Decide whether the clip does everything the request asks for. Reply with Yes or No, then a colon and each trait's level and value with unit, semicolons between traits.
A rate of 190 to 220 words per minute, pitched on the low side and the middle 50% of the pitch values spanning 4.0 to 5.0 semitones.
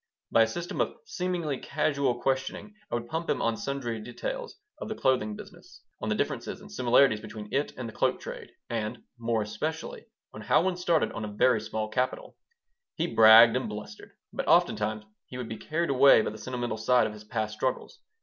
Yes: average, 195 wpm; low, 120 Hz; average, 4.4 semitones